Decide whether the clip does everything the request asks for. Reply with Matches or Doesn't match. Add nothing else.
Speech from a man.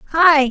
Doesn't match